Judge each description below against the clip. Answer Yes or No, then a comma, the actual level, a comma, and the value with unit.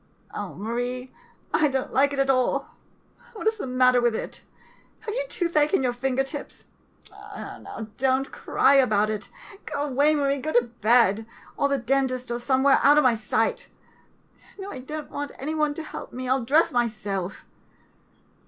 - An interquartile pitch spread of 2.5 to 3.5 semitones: Yes, average, 3.1 semitones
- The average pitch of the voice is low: No, very high, 265 Hz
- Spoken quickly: No, average, 185 wpm